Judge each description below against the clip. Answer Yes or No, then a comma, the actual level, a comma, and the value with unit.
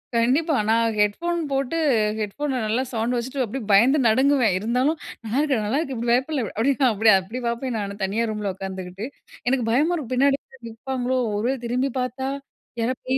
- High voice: Yes, high, 245 Hz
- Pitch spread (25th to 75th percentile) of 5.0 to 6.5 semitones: No, average, 3.6 semitones